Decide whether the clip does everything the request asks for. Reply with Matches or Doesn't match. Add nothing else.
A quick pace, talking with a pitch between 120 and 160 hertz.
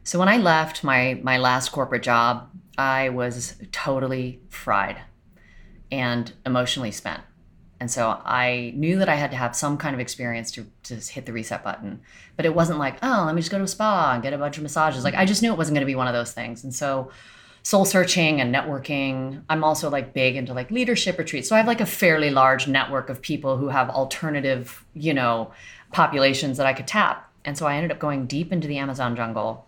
Matches